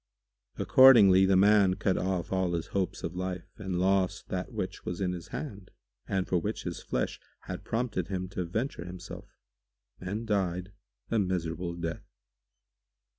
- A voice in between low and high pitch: No, very low, 95 Hz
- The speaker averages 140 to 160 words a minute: Yes, average, 155 wpm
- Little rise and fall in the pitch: Yes, narrow, 1.7 semitones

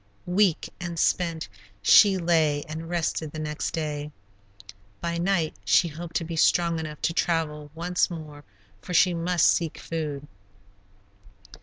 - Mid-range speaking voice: Yes, medium, 165 Hz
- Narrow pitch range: Yes, narrow, 2.1 semitones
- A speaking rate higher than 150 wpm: No, average, 140 wpm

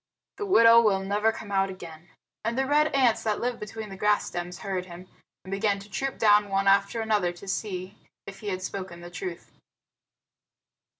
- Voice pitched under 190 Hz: No, high, 200 Hz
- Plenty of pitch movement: No, average, 2.9 semitones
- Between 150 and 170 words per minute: No, average, 190 wpm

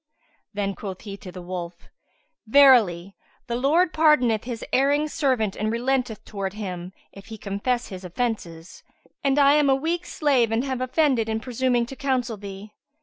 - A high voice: Yes, high, 235 Hz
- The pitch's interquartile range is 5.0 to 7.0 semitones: Yes, average, 5.3 semitones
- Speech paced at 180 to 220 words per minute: No, average, 165 wpm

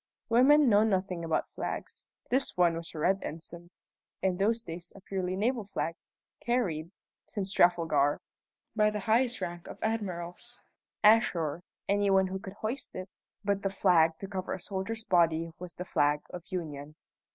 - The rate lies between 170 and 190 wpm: No, average, 160 wpm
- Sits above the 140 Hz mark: Yes, high, 190 Hz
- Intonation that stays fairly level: No, average, 3.8 semitones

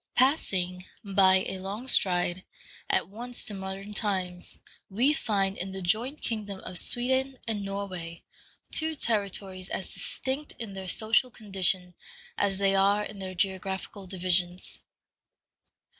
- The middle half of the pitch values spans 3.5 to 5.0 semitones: No, average, 2.7 semitones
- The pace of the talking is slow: Yes, slow, 130 wpm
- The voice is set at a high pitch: Yes, high, 195 Hz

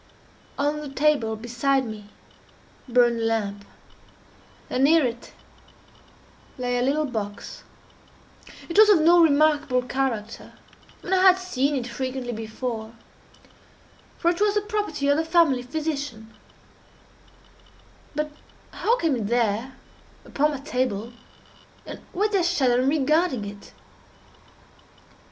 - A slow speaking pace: Yes, slow, 130 wpm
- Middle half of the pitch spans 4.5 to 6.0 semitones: Yes, average, 4.8 semitones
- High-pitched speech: Yes, very high, 270 Hz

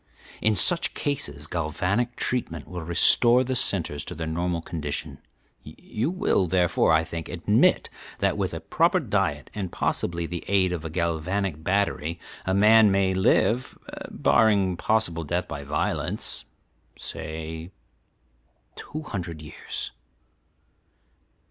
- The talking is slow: Yes, slow, 125 wpm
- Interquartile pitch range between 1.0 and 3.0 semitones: No, average, 4.4 semitones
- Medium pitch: No, very low, 90 Hz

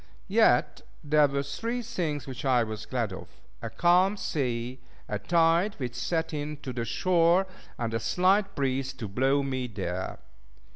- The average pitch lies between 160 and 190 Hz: No, medium, 140 Hz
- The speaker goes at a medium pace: Yes, average, 160 wpm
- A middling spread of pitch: No, wide, 5.7 semitones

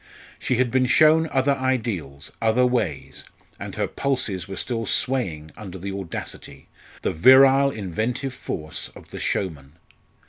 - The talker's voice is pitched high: No, low, 115 Hz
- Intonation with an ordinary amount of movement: No, wide, 6.7 semitones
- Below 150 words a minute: Yes, average, 140 wpm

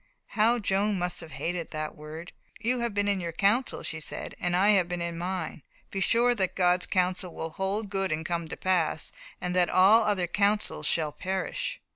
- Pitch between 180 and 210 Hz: Yes, medium, 185 Hz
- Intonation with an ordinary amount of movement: Yes, average, 3.0 semitones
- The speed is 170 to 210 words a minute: Yes, average, 200 wpm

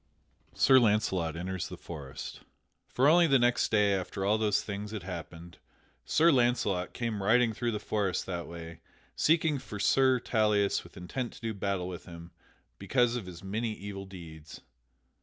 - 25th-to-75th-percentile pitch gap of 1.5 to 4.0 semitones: No, average, 4.9 semitones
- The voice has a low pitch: Yes, low, 100 Hz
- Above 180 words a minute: No, average, 170 wpm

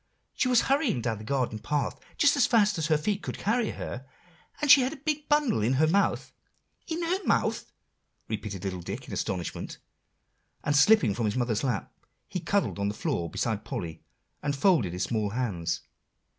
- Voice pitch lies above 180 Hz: No, medium, 140 Hz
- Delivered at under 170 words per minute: No, average, 185 wpm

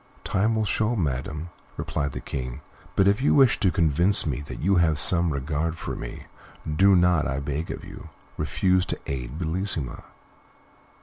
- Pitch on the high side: No, very low, 80 Hz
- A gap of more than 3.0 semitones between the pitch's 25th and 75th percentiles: Yes, average, 5.1 semitones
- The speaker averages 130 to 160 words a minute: No, average, 170 wpm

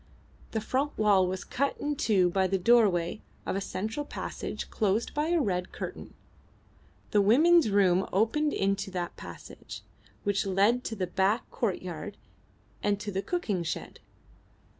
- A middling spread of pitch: Yes, average, 3.9 semitones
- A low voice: No, high, 205 Hz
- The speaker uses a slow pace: No, average, 150 wpm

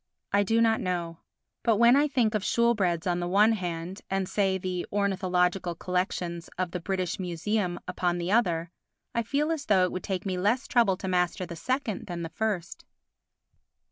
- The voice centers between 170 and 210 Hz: Yes, medium, 185 Hz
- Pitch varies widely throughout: No, average, 3.5 semitones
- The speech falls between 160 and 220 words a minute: Yes, average, 185 wpm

